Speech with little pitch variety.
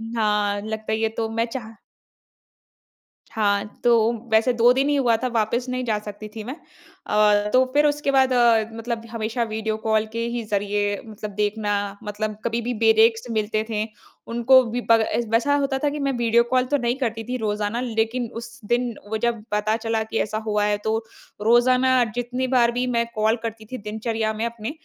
Yes: narrow, 2.0 semitones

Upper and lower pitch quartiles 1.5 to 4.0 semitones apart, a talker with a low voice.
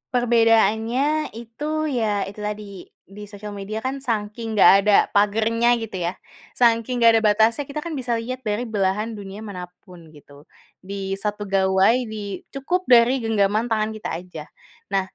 No: average, 2.8 semitones; high, 215 Hz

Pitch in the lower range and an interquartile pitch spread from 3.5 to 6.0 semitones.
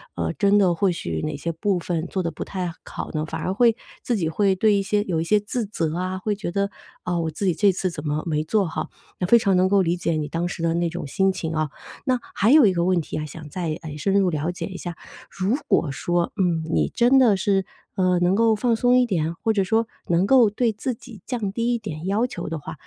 No: medium, 185 Hz; average, 3.9 semitones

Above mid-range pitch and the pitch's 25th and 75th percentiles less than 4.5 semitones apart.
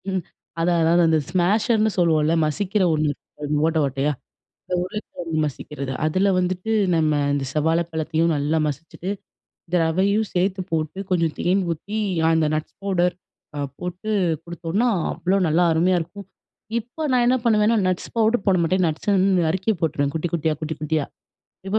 No: medium, 175 Hz; average, 3.4 semitones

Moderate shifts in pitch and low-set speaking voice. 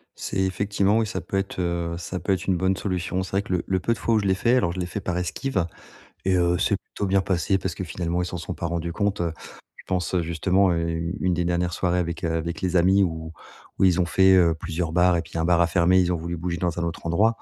No: narrow, 1.9 semitones; very low, 90 Hz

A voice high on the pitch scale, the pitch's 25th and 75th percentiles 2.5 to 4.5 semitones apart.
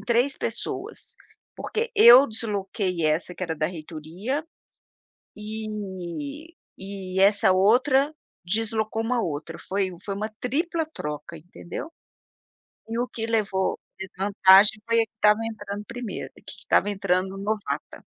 Yes: high, 210 Hz; average, 3.6 semitones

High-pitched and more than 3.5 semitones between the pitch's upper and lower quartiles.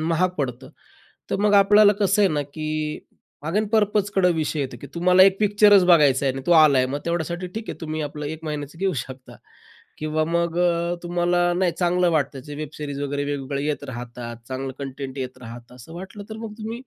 No: medium, 160 Hz; average, 4.6 semitones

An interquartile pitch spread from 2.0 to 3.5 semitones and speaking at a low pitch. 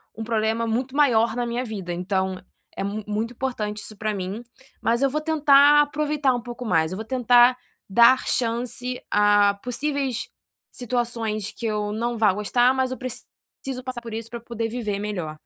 No: average, 3.2 semitones; high, 235 Hz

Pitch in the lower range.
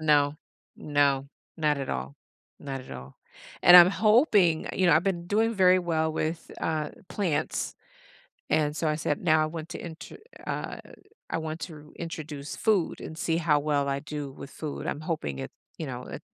No: medium, 155 Hz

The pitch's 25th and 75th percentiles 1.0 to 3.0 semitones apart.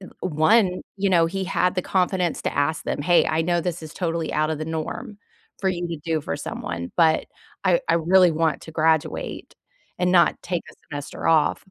Yes: narrow, 2.4 semitones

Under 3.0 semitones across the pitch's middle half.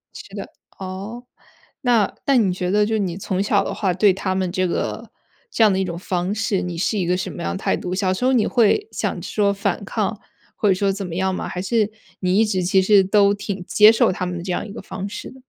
Yes: narrow, 2.4 semitones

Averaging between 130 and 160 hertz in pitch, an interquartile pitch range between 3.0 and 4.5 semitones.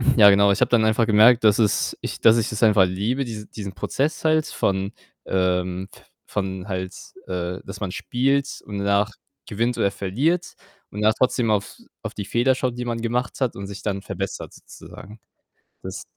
No: low, 105 Hz; average, 3.5 semitones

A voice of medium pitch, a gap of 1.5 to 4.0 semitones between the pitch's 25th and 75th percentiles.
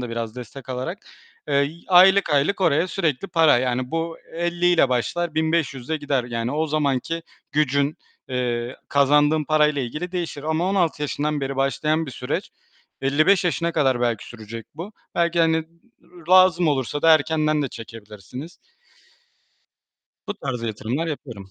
No: medium, 150 Hz; average, 4.5 semitones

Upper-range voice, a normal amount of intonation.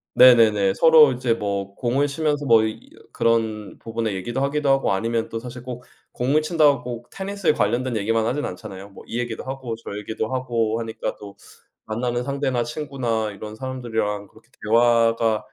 No: low, 120 Hz; average, 3.3 semitones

